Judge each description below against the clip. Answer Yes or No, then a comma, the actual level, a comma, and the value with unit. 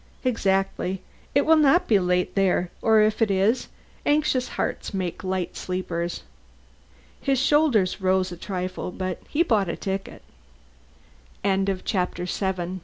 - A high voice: Yes, high, 195 Hz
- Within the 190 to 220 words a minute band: No, slow, 135 wpm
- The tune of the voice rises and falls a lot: No, average, 3.8 semitones